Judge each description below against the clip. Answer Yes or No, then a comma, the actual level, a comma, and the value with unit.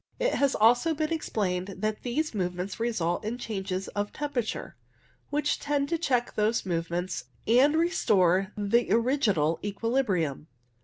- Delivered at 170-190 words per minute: No, average, 140 wpm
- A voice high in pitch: Yes, high, 220 Hz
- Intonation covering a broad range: Yes, wide, 6.7 semitones